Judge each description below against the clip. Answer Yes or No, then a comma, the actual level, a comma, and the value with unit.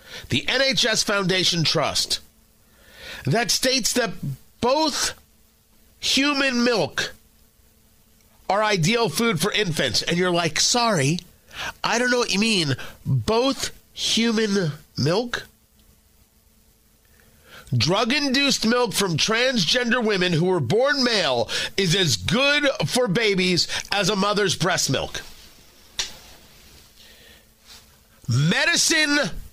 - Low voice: No, high, 200 Hz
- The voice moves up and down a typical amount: No, wide, 8.0 semitones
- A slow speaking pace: Yes, slow, 100 wpm